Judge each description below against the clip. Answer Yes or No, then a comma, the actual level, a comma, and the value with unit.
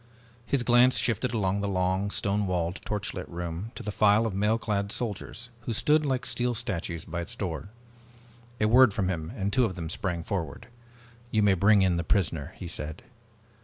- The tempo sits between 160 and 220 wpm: Yes, average, 190 wpm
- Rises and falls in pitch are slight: No, average, 4.1 semitones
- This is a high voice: No, low, 100 Hz